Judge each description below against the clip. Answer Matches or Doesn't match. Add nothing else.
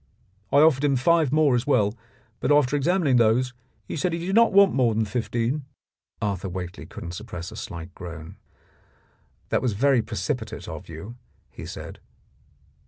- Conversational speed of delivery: Matches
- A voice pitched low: Matches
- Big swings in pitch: Matches